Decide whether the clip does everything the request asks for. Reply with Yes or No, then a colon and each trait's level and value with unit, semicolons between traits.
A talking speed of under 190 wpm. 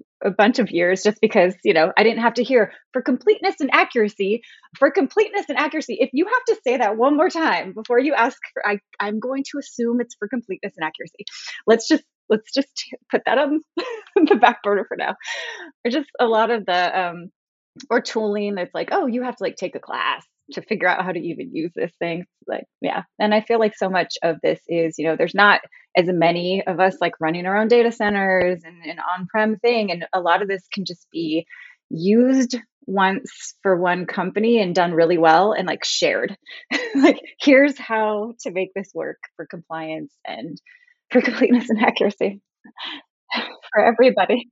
No: average, 200 wpm